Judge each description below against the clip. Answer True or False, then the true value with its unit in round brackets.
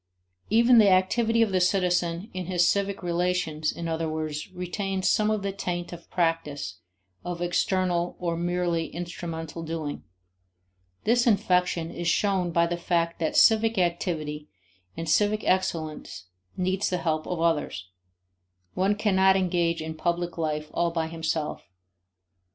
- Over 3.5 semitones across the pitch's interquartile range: False (2.4 semitones)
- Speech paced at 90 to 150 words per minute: True (140 wpm)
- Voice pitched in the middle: True (175 Hz)